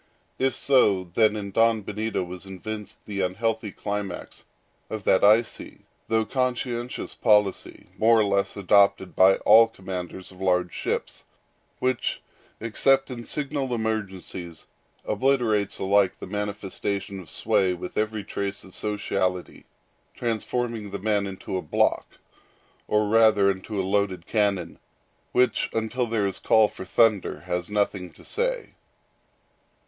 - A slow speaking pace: Yes, slow, 130 wpm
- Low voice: Yes, low, 105 Hz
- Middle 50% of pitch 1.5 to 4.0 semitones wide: Yes, average, 2.9 semitones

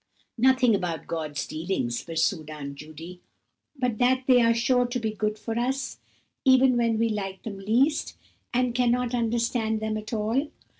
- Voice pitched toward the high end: Yes, high, 225 Hz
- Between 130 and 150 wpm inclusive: No, average, 160 wpm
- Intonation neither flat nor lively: Yes, average, 4.5 semitones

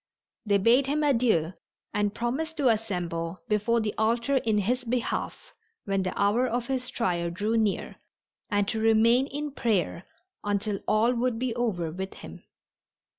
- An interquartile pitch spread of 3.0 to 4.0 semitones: Yes, average, 3.7 semitones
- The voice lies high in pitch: Yes, high, 225 Hz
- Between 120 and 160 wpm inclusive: Yes, average, 155 wpm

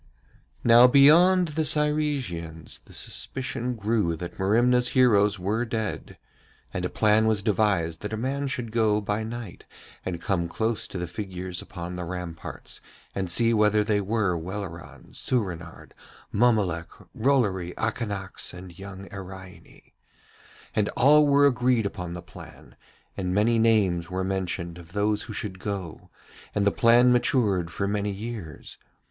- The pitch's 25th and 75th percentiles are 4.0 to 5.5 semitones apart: Yes, average, 4.4 semitones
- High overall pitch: No, low, 105 Hz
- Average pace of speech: Yes, average, 145 wpm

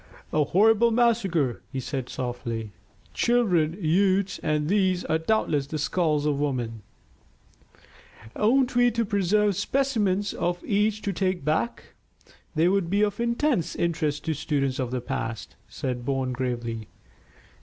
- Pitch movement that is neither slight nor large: No, wide, 7.1 semitones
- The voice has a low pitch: No, medium, 170 Hz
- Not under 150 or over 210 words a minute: No, slow, 135 wpm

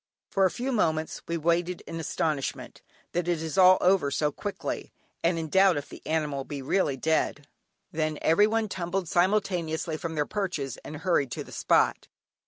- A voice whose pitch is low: No, medium, 165 Hz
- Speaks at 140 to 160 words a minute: No, average, 175 wpm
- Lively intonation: No, average, 3.2 semitones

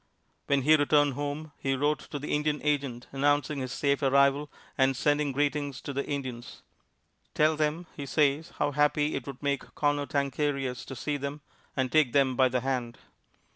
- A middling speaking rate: Yes, average, 175 wpm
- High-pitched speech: No, medium, 140 Hz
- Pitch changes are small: Yes, narrow, 1.6 semitones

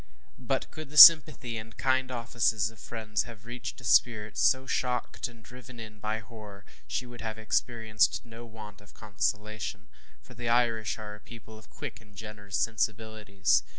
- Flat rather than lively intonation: Yes, narrow, 2.1 semitones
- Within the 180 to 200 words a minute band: No, average, 170 wpm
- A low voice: Yes, low, 110 Hz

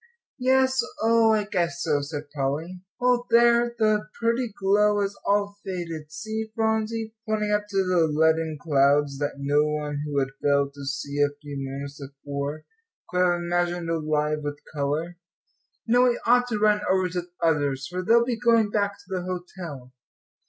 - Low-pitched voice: No, medium, 175 Hz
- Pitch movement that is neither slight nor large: No, wide, 6.6 semitones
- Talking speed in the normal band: Yes, average, 170 wpm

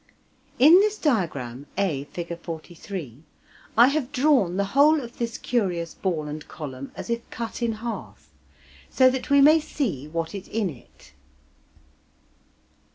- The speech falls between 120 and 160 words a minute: Yes, average, 145 wpm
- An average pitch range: No, wide, 8.4 semitones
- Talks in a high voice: Yes, high, 200 Hz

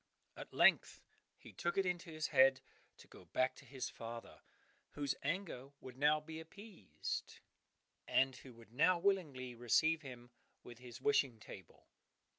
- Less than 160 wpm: Yes, average, 150 wpm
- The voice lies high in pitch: No, low, 135 Hz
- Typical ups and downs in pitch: Yes, average, 4.7 semitones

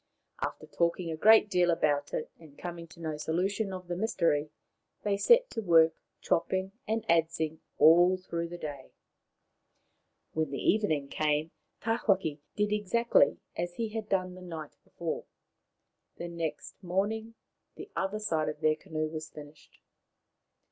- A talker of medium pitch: Yes, medium, 170 Hz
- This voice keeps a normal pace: Yes, average, 150 wpm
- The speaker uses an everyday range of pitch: Yes, average, 4.1 semitones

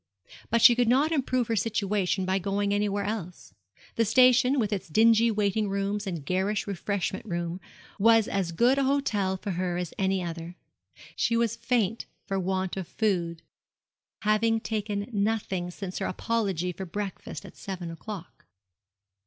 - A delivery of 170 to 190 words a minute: No, average, 155 wpm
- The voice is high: Yes, high, 200 Hz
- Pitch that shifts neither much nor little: Yes, average, 3.4 semitones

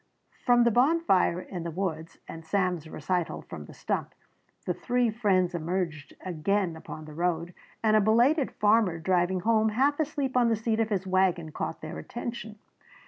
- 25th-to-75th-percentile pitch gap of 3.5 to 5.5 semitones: Yes, average, 5.1 semitones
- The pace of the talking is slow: No, average, 170 wpm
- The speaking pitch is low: No, high, 190 Hz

